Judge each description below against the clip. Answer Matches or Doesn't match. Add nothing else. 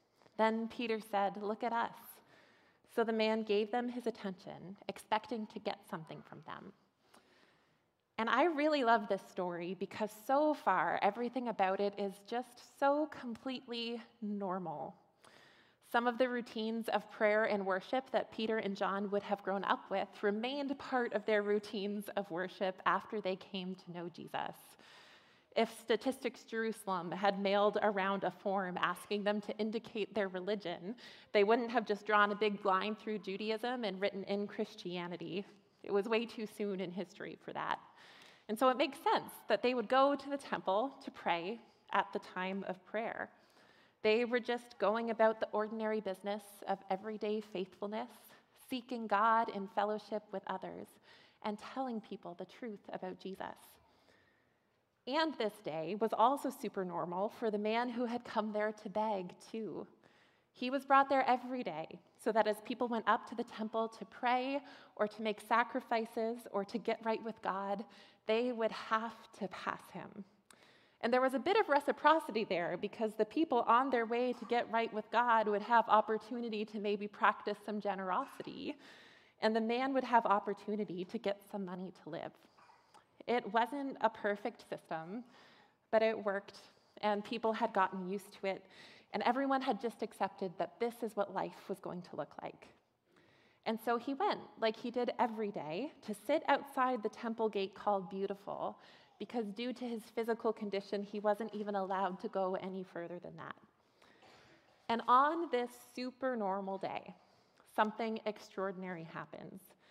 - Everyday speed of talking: Matches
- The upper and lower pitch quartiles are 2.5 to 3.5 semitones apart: Matches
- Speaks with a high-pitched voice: Matches